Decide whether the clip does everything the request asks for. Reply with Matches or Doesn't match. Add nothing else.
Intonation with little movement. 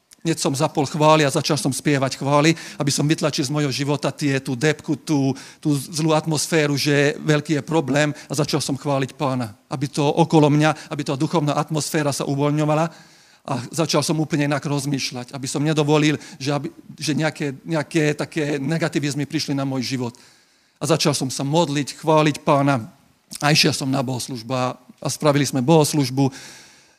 Matches